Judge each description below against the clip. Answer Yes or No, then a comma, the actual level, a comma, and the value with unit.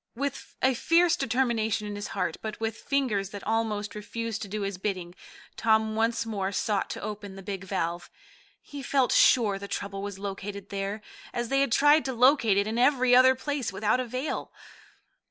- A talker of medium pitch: No, high, 220 Hz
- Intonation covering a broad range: No, average, 4.1 semitones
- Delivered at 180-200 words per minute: Yes, average, 185 wpm